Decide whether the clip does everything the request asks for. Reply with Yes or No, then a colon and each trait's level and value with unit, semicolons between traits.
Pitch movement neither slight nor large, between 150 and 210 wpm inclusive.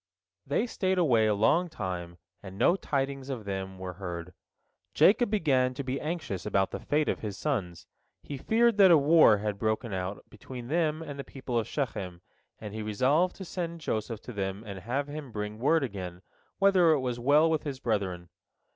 No: wide, 7.4 semitones; average, 190 wpm